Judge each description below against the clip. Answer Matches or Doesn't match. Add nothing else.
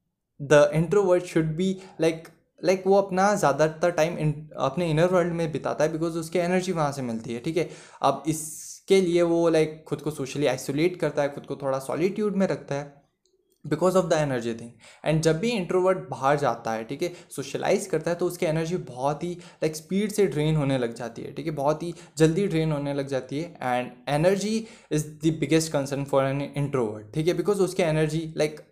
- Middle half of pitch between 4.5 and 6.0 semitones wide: Doesn't match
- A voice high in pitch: Doesn't match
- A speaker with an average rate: Doesn't match